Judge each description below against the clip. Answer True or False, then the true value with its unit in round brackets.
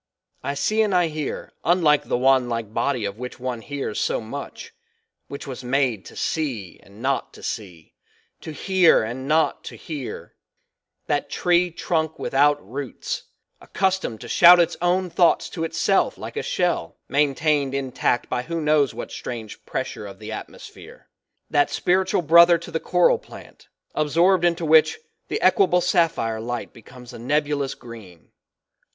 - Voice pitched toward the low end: False (145 Hz)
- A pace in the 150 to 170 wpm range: True (155 wpm)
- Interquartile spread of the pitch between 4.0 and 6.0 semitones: True (5.6 semitones)